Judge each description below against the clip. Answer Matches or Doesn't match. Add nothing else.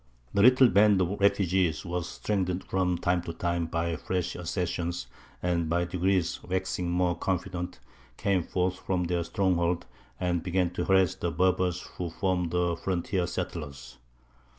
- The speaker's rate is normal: Matches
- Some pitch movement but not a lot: Doesn't match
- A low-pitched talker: Matches